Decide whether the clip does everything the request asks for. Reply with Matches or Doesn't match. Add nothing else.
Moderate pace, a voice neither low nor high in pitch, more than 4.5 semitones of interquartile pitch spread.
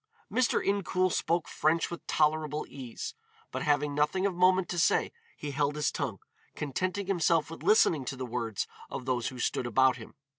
Matches